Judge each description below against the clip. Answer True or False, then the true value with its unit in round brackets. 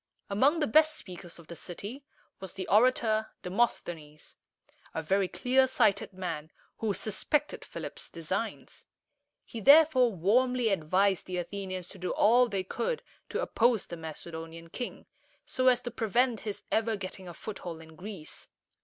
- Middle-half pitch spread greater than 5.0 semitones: True (5.5 semitones)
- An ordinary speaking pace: True (155 wpm)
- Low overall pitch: False (200 Hz)